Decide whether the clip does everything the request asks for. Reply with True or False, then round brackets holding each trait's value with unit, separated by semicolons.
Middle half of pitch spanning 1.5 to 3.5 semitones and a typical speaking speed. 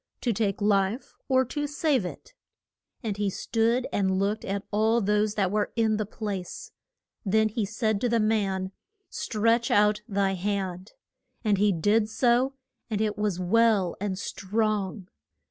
True (2.4 semitones; 155 wpm)